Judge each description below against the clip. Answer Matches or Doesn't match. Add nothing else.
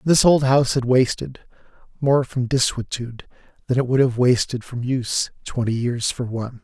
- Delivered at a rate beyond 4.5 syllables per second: Matches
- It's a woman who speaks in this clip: Doesn't match